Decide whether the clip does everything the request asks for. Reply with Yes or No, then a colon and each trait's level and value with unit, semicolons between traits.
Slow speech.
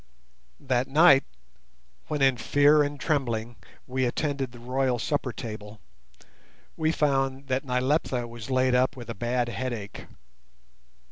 Yes: slow, 130 wpm